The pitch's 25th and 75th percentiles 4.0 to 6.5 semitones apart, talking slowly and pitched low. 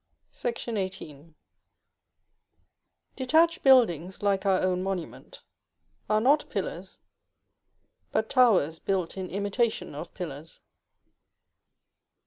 No: average, 5.2 semitones; slow, 90 wpm; high, 195 Hz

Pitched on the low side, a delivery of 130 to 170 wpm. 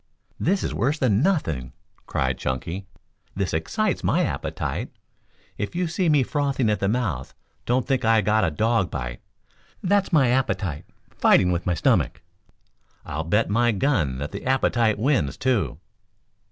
Yes: low, 110 Hz; average, 155 wpm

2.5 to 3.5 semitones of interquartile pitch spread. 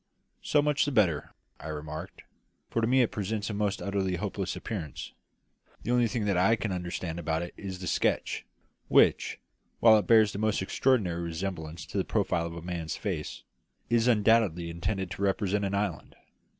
No: average, 4.2 semitones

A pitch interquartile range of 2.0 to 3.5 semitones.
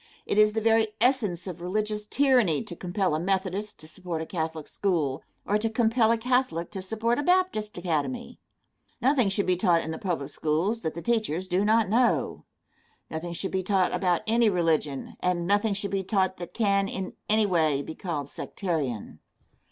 No: average, 4.4 semitones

